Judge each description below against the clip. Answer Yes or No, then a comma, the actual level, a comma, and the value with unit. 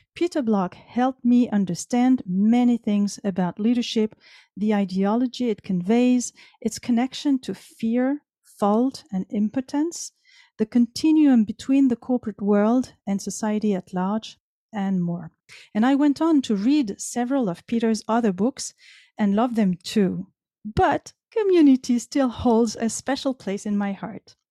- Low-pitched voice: No, high, 230 Hz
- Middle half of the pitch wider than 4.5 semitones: No, average, 3.9 semitones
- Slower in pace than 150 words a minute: Yes, average, 140 wpm